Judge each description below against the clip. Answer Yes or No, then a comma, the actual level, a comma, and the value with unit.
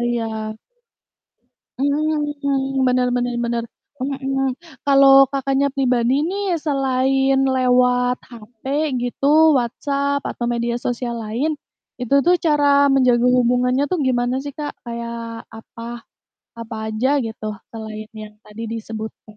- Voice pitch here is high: Yes, very high, 250 Hz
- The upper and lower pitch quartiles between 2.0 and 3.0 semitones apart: Yes, average, 2.7 semitones